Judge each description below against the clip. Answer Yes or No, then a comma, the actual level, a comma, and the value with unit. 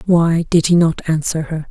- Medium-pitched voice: Yes, medium, 165 Hz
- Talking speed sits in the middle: No, fast, 210 wpm